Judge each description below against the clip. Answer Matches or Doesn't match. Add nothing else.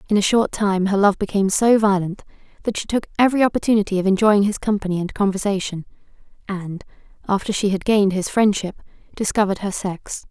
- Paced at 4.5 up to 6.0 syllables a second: Doesn't match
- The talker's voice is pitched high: Matches